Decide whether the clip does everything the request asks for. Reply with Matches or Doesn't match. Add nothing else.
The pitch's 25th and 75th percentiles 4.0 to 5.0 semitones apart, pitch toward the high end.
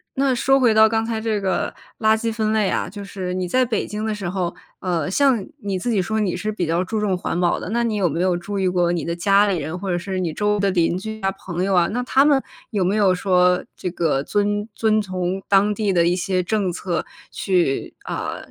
Doesn't match